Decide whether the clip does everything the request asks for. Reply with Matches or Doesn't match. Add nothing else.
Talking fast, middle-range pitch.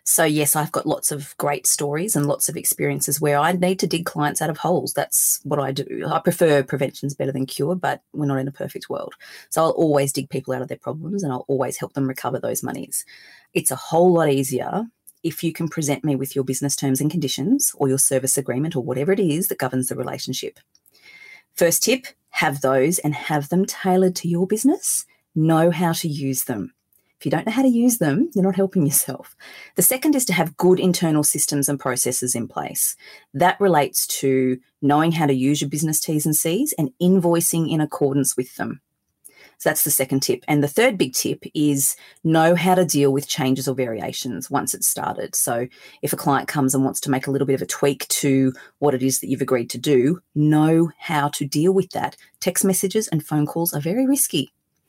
Matches